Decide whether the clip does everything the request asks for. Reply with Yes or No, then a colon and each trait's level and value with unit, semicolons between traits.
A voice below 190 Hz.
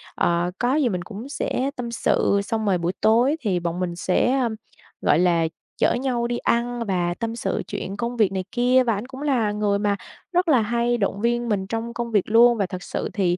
No: high, 225 Hz